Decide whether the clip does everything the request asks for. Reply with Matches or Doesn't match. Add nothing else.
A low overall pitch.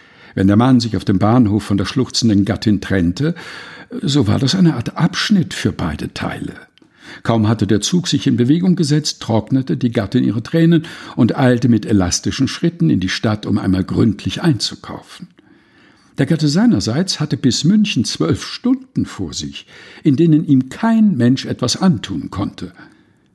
Matches